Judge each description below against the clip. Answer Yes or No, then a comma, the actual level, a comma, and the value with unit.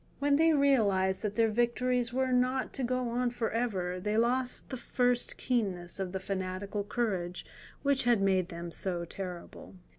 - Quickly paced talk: No, average, 170 wpm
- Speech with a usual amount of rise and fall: Yes, average, 4.9 semitones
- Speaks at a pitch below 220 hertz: No, high, 225 Hz